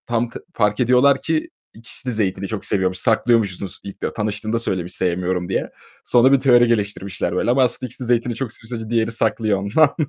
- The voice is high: No, low, 115 Hz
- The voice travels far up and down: No, average, 3.5 semitones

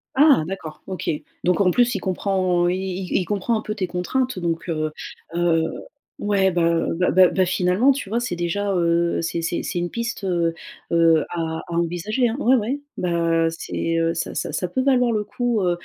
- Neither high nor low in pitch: Yes, medium, 180 Hz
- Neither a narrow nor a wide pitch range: Yes, average, 3.8 semitones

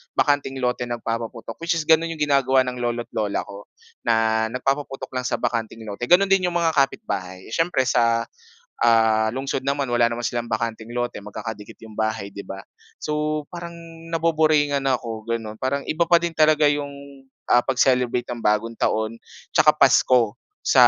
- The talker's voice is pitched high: No, low, 125 Hz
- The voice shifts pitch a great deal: No, average, 4.5 semitones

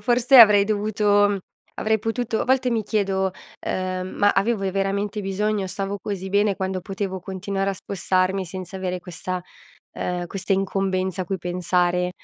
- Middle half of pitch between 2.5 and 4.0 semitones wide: No, narrow, 1.8 semitones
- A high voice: Yes, high, 195 Hz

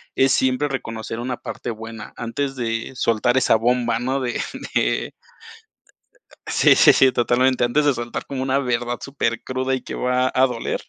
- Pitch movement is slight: Yes, narrow, 2.0 semitones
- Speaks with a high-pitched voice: No, low, 125 Hz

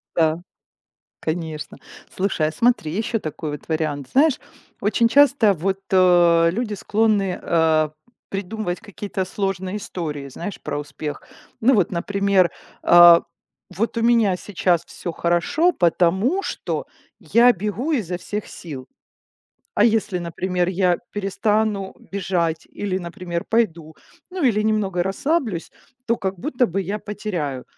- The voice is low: No, high, 190 Hz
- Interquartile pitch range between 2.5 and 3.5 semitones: No, average, 4.1 semitones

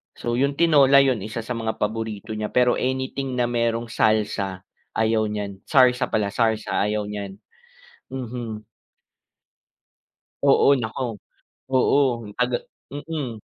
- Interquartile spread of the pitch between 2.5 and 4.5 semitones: Yes, average, 3.1 semitones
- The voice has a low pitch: Yes, low, 115 Hz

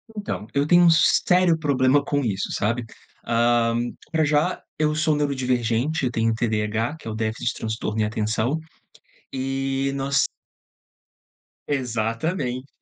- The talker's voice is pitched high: No, low, 130 Hz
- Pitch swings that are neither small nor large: Yes, average, 4.6 semitones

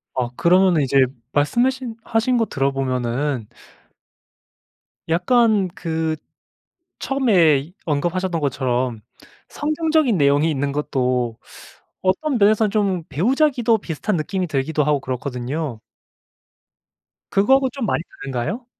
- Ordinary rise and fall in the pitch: No, wide, 8.3 semitones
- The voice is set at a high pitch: No, medium, 165 Hz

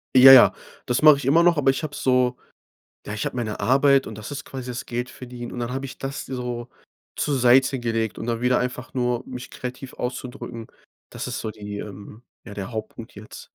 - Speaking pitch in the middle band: No, low, 125 Hz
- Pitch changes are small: Yes, narrow, 2.3 semitones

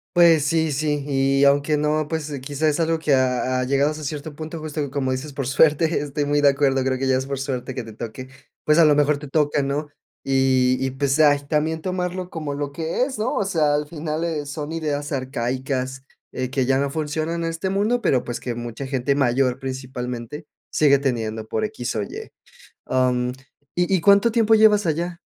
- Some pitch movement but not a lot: Yes, average, 3.3 semitones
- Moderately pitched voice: Yes, medium, 145 Hz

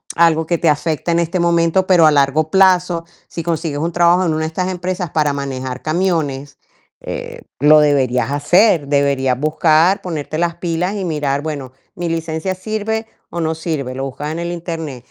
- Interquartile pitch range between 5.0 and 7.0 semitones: No, average, 3.1 semitones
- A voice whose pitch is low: No, medium, 160 Hz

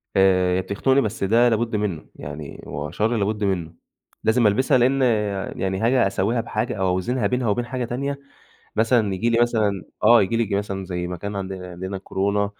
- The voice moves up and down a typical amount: Yes, average, 3.8 semitones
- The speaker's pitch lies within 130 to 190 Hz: No, low, 105 Hz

